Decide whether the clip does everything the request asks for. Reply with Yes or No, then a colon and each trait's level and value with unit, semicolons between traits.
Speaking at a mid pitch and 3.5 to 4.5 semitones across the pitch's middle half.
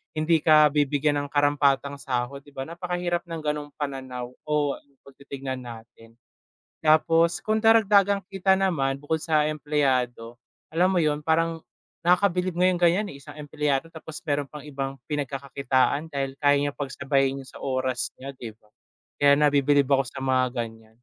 No: medium, 145 Hz; average, 3.1 semitones